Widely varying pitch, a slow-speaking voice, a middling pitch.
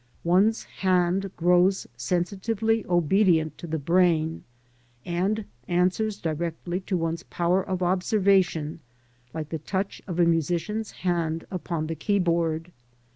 No: narrow, 2.6 semitones; slow, 120 wpm; medium, 175 Hz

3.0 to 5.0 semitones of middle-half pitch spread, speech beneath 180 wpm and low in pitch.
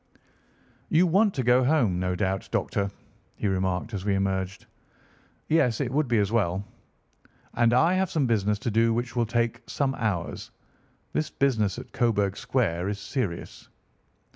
Yes: average, 4.7 semitones; average, 160 wpm; low, 115 Hz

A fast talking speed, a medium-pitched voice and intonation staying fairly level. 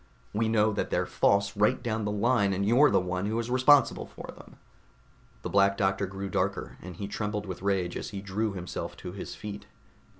No: fast, 210 wpm; low, 100 Hz; narrow, 2.1 semitones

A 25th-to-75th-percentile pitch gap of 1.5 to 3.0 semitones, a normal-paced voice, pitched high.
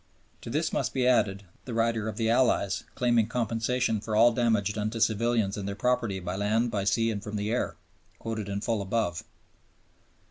No: narrow, 2.5 semitones; average, 190 wpm; low, 110 Hz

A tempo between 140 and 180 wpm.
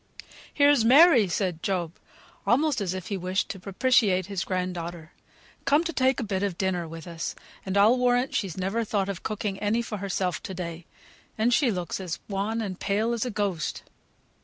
No: average, 190 wpm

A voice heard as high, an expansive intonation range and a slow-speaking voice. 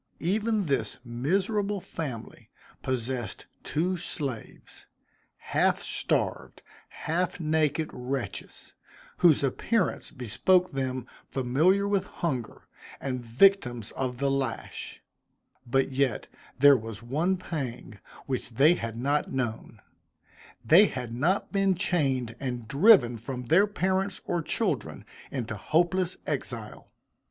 No: medium, 140 Hz; wide, 6.6 semitones; slow, 110 wpm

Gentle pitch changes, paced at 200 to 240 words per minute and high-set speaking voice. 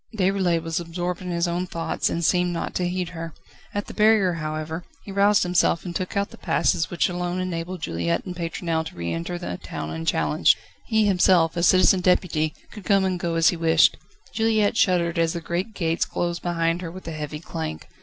No: narrow, 2.0 semitones; fast, 205 wpm; medium, 175 Hz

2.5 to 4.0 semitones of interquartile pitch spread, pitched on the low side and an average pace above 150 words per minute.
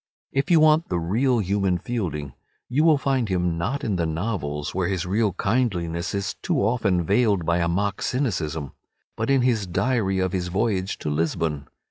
No: wide, 5.6 semitones; very low, 95 Hz; average, 180 wpm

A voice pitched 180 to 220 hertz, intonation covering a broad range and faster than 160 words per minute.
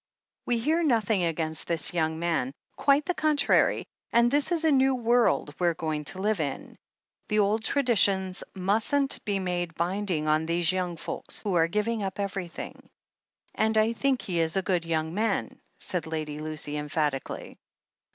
Yes: high, 190 Hz; wide, 5.8 semitones; average, 170 wpm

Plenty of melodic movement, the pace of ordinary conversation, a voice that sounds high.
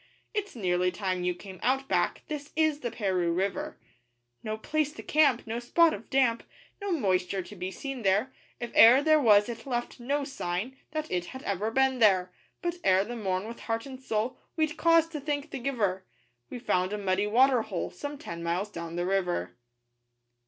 Yes: wide, 6.6 semitones; average, 195 wpm; high, 230 Hz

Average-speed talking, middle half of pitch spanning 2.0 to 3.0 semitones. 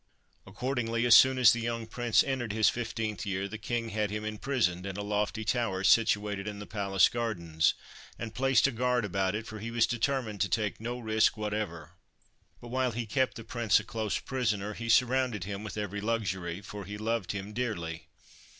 Yes: average, 195 wpm; narrow, 2.6 semitones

